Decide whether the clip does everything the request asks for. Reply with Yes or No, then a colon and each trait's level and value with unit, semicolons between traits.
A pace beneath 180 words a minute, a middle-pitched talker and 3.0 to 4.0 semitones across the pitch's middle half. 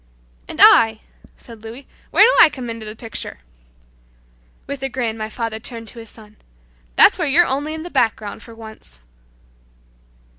No: average, 170 wpm; high, 230 Hz; average, 3.5 semitones